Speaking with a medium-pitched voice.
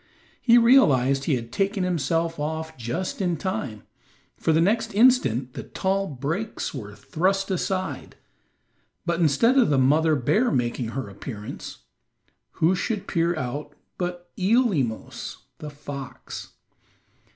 Yes: medium, 160 Hz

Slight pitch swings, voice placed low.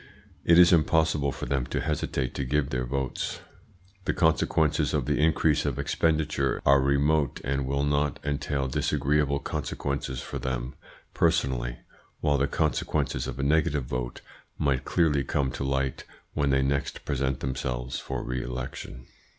Yes: narrow, 2.1 semitones; very low, 70 Hz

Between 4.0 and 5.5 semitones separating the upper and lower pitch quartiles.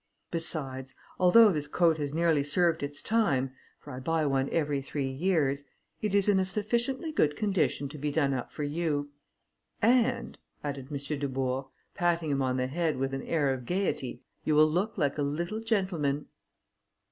Yes: average, 4.5 semitones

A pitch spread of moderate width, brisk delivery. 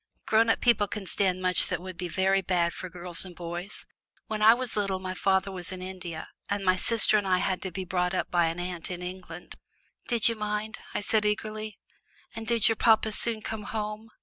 Yes: average, 3.0 semitones; fast, 220 wpm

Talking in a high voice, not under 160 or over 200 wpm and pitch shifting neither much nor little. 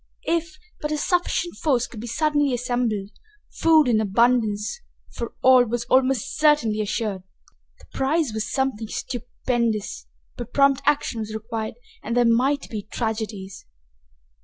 No: high, 240 Hz; slow, 135 wpm; average, 4.1 semitones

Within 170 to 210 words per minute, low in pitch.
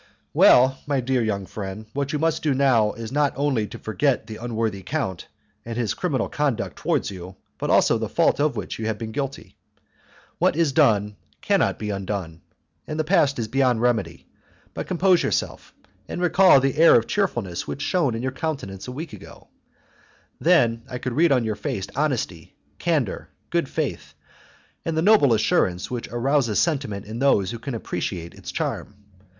Yes: average, 180 wpm; low, 125 Hz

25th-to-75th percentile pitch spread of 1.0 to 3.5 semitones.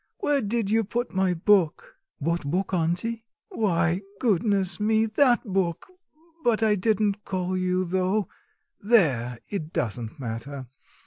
No: average, 4.5 semitones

